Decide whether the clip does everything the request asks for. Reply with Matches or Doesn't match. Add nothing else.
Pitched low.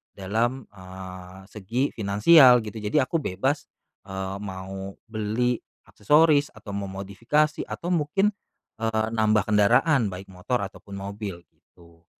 Matches